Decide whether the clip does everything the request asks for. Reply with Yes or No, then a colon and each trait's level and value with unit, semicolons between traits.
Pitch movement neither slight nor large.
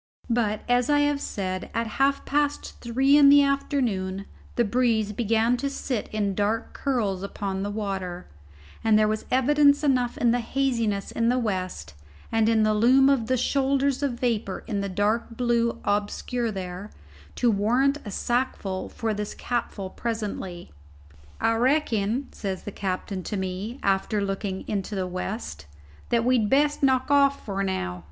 Yes: average, 4.5 semitones